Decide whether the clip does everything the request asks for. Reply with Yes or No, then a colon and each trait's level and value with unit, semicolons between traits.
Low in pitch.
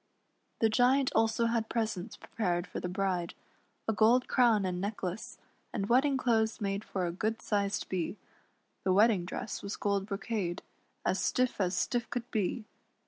No: high, 215 Hz